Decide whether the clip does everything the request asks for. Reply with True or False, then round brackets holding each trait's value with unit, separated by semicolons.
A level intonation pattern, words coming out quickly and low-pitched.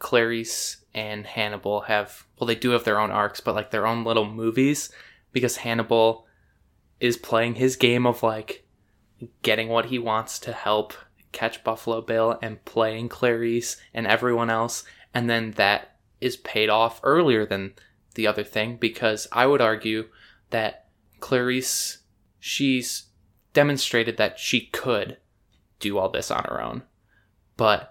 False (1.9 semitones; 150 wpm; 115 Hz)